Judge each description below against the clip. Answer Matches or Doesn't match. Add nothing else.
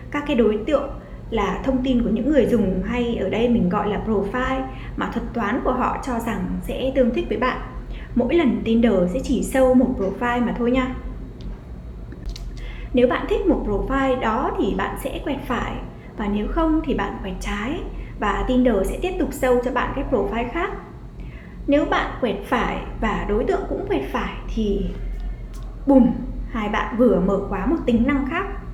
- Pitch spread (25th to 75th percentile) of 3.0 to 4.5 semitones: Matches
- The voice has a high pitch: Matches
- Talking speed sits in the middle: Matches